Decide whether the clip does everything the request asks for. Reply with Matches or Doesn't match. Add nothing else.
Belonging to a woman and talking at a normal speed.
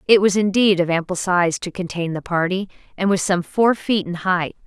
Doesn't match